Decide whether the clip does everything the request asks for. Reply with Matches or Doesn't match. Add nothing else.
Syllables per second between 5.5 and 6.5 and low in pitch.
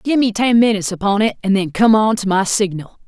Doesn't match